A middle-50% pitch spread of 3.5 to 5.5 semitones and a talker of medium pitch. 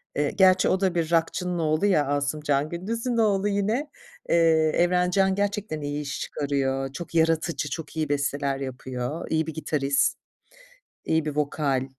Yes: average, 4.5 semitones; medium, 160 Hz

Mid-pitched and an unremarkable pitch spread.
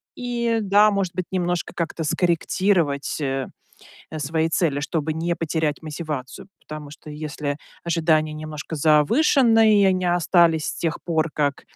Yes: medium, 160 Hz; average, 3.2 semitones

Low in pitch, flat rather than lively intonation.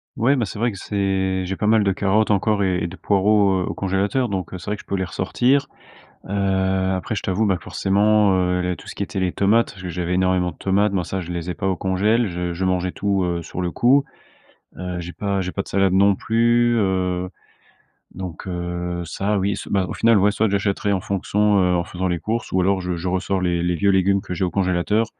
Yes: very low, 95 Hz; narrow, 2.1 semitones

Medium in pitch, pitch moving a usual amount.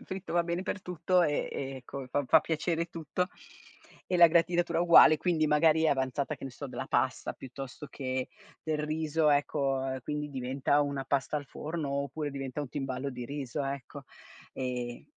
Yes: medium, 145 Hz; average, 3.1 semitones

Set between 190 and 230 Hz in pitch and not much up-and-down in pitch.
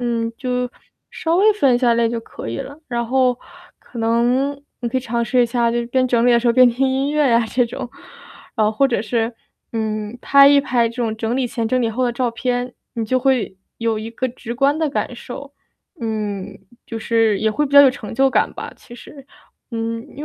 No: high, 240 Hz; narrow, 2.3 semitones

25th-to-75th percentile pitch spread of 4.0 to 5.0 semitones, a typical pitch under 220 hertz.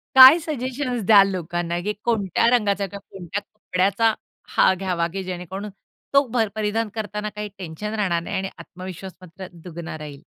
No: average, 3.4 semitones; high, 195 Hz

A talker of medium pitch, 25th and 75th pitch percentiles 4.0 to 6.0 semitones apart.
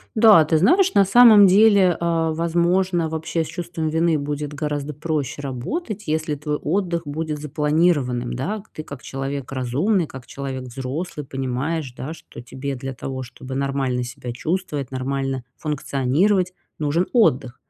Yes: medium, 150 Hz; average, 4.3 semitones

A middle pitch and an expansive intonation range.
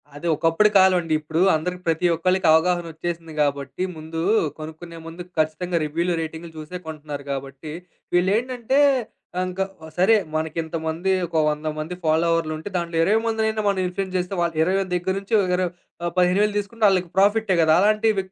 No: medium, 175 Hz; average, 3.1 semitones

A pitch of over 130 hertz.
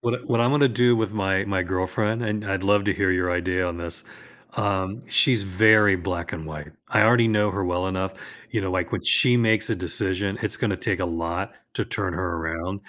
No: very low, 95 Hz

